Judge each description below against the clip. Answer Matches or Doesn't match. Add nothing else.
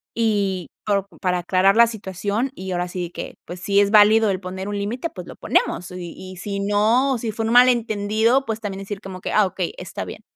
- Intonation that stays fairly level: Doesn't match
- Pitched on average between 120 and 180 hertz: Doesn't match